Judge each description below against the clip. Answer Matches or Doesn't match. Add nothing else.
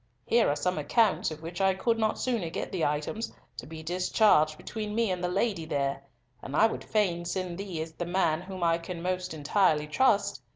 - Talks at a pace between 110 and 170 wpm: Doesn't match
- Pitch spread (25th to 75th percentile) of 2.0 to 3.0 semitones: Doesn't match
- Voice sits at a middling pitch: Matches